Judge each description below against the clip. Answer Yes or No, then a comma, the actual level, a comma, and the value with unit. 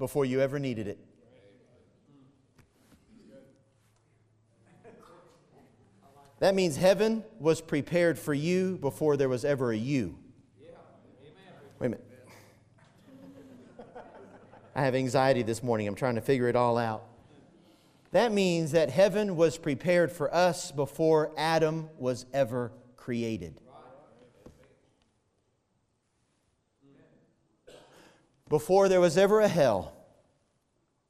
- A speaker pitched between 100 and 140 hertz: Yes, low, 135 Hz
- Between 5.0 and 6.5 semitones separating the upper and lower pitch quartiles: Yes, wide, 5.5 semitones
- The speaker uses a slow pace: Yes, slow, 100 wpm